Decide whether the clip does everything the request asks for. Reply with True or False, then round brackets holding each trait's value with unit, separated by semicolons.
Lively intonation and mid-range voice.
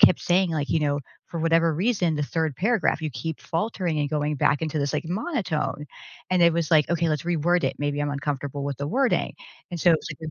False (3.0 semitones; 160 Hz)